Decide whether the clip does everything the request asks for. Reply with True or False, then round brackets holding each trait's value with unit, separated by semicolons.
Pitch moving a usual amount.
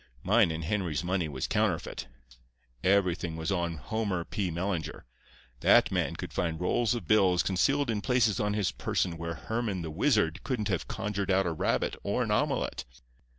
True (4.1 semitones)